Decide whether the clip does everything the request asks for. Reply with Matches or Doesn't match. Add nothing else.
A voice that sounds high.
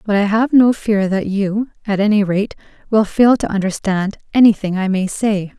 Matches